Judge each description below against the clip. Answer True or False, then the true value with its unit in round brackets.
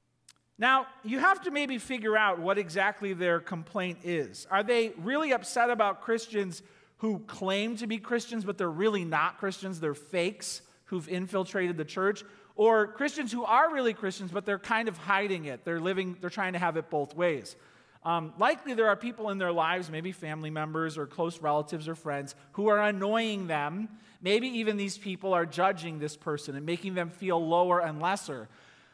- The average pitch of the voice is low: False (190 Hz)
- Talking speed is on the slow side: False (185 wpm)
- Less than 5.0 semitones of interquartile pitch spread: True (4.3 semitones)